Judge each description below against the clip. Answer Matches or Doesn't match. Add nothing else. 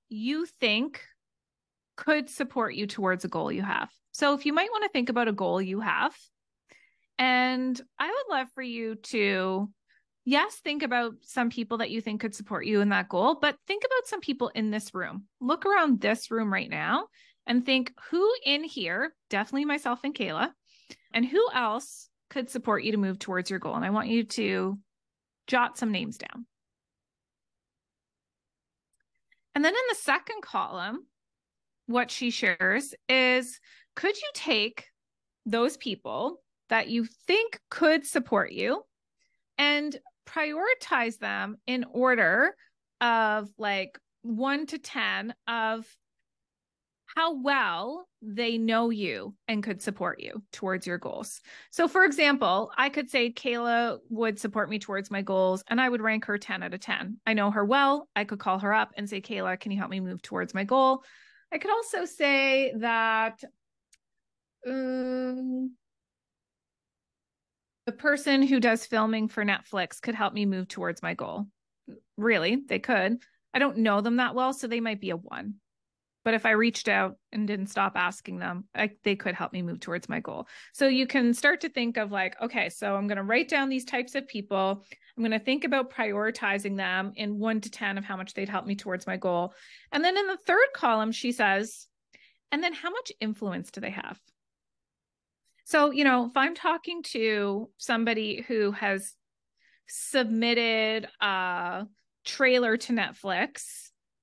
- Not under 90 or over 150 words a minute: Doesn't match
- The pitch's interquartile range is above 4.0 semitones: Matches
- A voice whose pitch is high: Matches